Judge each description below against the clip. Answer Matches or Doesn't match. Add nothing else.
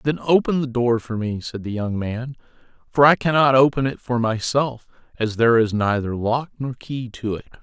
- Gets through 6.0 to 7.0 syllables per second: Doesn't match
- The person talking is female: Doesn't match